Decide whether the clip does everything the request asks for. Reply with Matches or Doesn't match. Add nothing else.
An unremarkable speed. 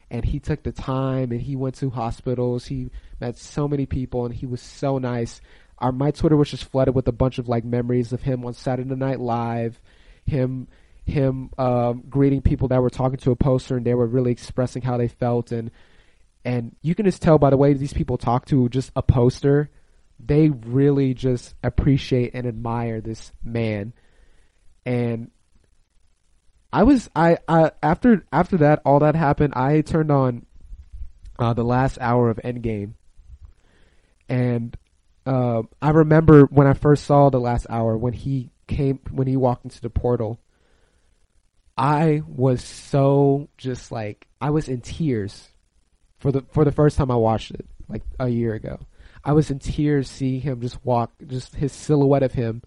Matches